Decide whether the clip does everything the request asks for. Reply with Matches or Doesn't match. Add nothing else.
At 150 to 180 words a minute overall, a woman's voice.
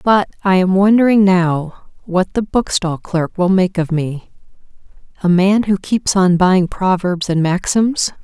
Matches